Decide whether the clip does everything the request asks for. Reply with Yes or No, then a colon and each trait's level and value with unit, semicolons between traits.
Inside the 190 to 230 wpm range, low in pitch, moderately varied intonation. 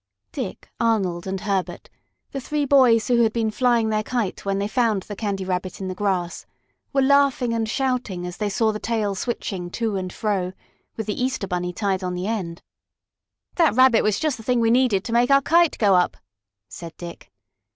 No: average, 195 wpm; high, 215 Hz; average, 4.4 semitones